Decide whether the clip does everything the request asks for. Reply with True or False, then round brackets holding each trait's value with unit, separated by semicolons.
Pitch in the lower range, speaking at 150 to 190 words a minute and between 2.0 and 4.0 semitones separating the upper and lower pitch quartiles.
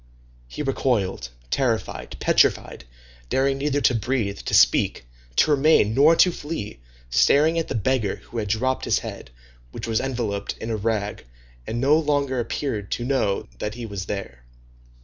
False (120 Hz; 160 wpm; 5.1 semitones)